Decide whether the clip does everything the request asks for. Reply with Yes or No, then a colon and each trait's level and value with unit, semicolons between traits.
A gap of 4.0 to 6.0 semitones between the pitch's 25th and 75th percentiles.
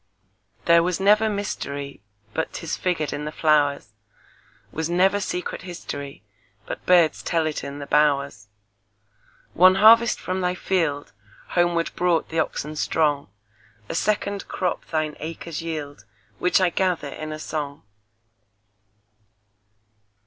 Yes: average, 4.3 semitones